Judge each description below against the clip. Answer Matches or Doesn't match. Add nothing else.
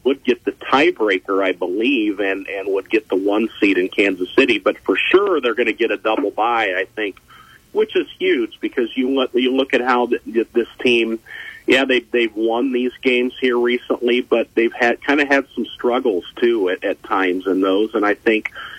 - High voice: Doesn't match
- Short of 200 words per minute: Doesn't match